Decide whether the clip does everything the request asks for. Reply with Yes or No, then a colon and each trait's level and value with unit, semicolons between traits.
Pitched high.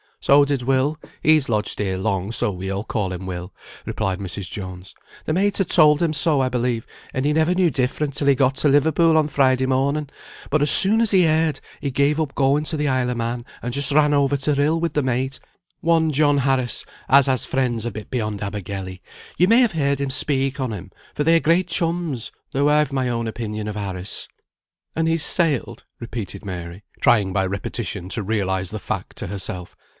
No: low, 135 Hz